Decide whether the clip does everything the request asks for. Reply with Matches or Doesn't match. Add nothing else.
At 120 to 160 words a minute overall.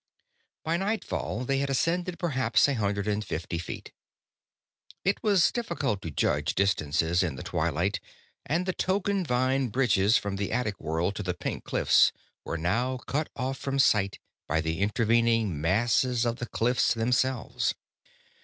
Matches